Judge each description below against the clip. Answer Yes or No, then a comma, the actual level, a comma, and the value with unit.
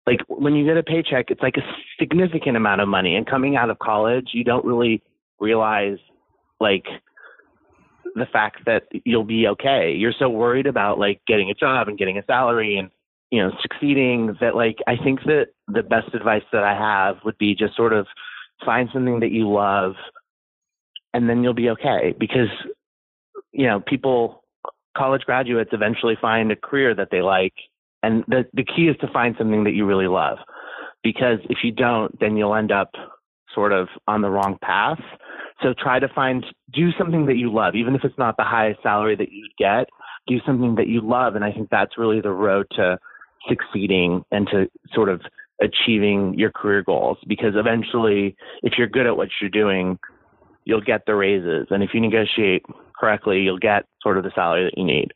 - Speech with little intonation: No, average, 3.8 semitones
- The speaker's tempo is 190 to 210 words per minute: Yes, average, 195 wpm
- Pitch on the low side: Yes, low, 115 Hz